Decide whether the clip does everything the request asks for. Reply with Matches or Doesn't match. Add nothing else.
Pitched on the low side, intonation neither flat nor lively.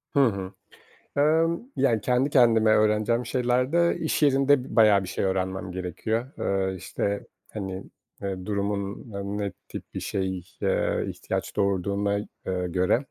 Matches